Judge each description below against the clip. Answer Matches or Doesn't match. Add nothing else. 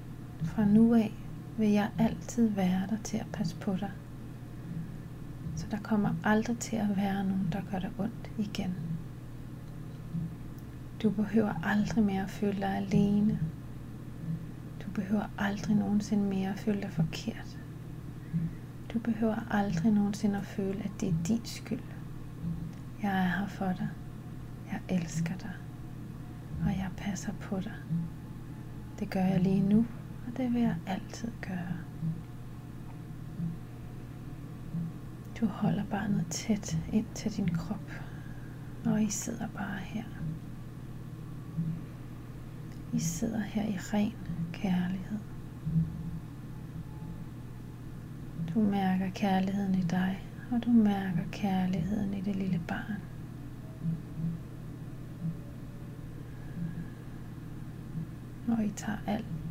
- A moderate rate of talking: Doesn't match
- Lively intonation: Matches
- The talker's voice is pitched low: Doesn't match